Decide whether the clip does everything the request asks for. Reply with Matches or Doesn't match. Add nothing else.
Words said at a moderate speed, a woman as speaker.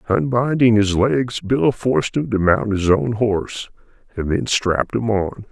Doesn't match